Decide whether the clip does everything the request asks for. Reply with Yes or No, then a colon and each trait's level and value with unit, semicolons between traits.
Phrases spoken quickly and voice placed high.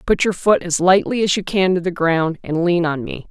No: fast, 270 wpm; medium, 180 Hz